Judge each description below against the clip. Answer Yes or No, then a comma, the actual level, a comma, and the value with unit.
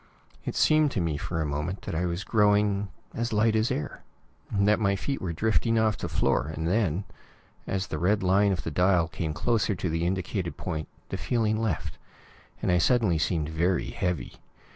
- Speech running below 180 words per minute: No, average, 190 wpm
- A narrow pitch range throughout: No, average, 4.2 semitones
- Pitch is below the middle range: Yes, very low, 95 Hz